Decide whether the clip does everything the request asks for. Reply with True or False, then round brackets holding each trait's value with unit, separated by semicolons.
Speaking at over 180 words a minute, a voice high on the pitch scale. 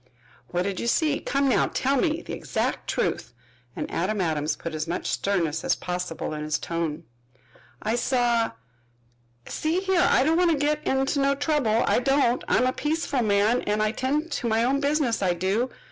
True (190 wpm; 240 Hz)